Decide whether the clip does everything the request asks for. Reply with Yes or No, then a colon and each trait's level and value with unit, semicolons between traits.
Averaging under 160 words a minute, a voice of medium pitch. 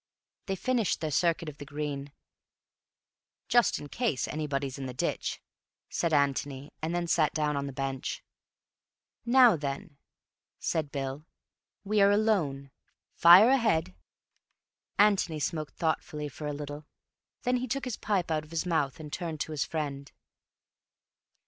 Yes: average, 140 wpm; medium, 155 Hz